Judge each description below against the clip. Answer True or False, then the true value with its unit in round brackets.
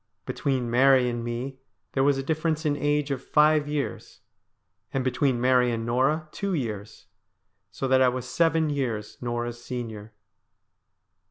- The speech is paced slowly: False (150 wpm)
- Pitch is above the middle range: False (130 Hz)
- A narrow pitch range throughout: False (3.5 semitones)